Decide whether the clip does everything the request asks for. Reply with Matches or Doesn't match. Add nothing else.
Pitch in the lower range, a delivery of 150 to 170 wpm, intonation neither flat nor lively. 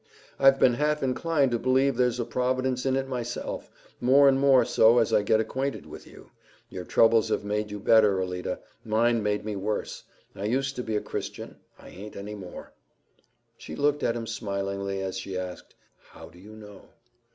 Doesn't match